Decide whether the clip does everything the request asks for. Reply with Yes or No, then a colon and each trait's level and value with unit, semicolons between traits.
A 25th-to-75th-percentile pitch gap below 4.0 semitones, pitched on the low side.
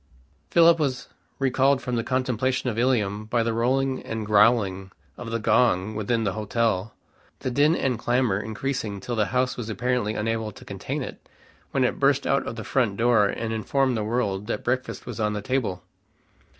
Yes: average, 3.2 semitones; low, 115 Hz